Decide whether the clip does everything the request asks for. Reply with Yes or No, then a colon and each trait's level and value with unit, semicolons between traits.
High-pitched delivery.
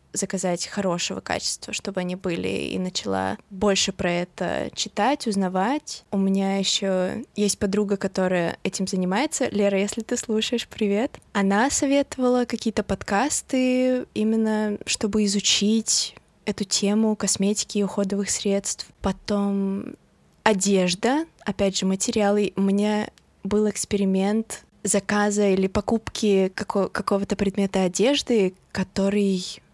Yes: high, 205 Hz